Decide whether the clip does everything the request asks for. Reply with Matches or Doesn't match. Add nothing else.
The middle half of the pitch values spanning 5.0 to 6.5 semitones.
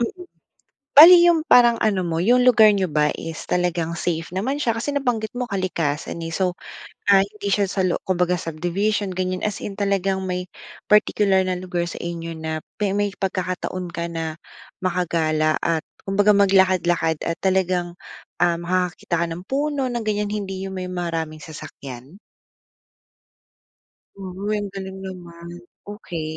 Doesn't match